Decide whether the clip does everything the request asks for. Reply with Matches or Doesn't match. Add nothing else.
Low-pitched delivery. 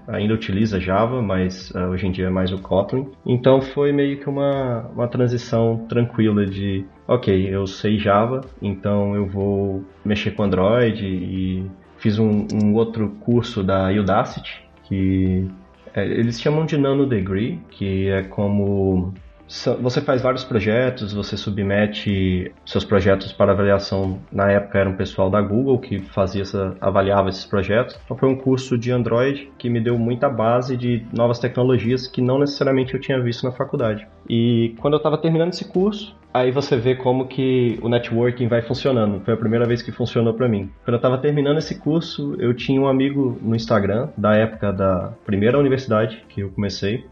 Matches